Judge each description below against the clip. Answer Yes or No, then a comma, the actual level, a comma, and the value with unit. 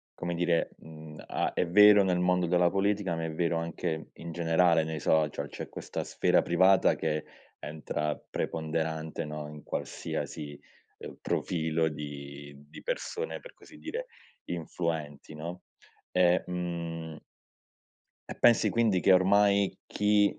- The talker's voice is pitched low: Yes, very low, 85 Hz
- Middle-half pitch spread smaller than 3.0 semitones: Yes, narrow, 2.6 semitones